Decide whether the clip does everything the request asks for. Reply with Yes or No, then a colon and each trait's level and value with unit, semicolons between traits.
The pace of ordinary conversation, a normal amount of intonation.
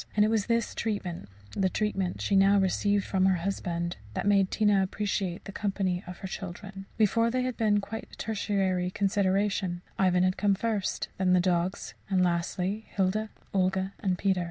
No: average, 180 wpm; narrow, 2.0 semitones